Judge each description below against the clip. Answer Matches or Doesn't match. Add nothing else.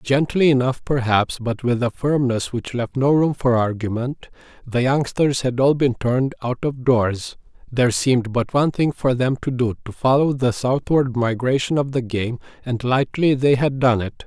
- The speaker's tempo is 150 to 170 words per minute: Doesn't match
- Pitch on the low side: Matches